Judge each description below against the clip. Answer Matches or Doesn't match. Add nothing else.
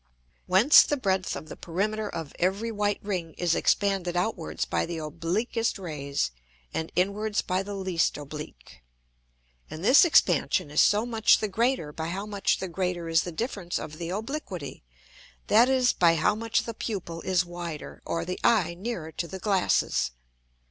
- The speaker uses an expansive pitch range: Doesn't match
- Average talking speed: Matches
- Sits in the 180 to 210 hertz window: Matches